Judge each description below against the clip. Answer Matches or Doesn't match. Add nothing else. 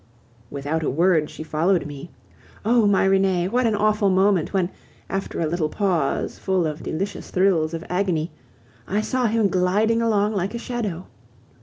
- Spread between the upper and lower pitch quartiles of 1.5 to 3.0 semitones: Doesn't match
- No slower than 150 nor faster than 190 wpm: Matches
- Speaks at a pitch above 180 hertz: Matches